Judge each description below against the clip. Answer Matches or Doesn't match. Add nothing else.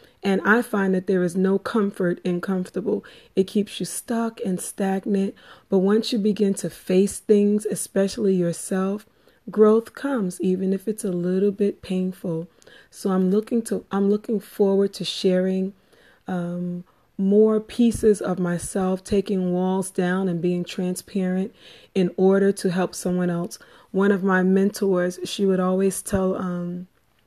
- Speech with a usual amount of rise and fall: Doesn't match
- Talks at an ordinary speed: Matches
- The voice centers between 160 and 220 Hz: Matches